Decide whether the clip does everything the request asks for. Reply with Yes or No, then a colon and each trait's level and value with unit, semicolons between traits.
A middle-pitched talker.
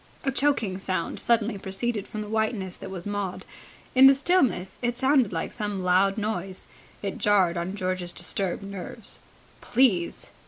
No: high, 200 Hz